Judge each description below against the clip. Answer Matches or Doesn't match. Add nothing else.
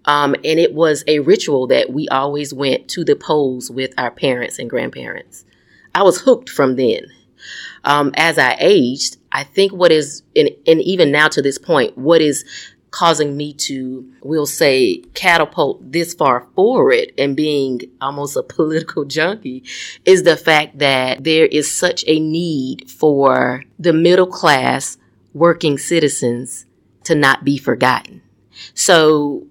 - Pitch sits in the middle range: Matches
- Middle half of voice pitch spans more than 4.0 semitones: Doesn't match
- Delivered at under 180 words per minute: Matches